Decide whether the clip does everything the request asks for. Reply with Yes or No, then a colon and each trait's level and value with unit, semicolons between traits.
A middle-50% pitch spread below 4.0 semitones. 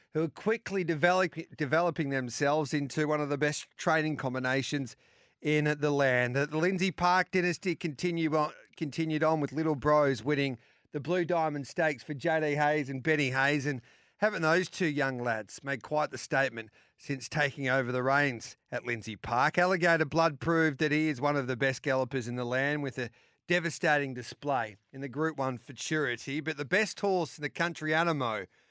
Yes: average, 3.2 semitones